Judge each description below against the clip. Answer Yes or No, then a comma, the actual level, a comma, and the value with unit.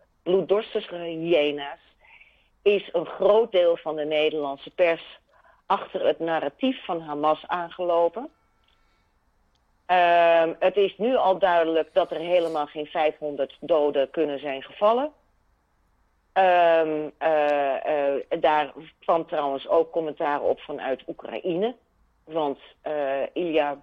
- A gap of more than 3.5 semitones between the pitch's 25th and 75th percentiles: No, average, 3.2 semitones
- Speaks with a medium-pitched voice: Yes, medium, 160 Hz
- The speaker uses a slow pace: Yes, slow, 115 wpm